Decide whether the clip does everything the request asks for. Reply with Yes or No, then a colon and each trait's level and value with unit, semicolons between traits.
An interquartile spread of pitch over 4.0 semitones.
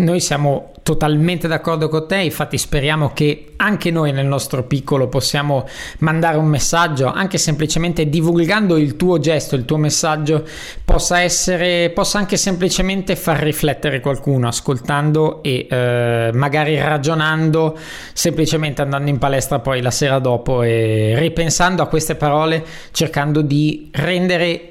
No: average, 2.9 semitones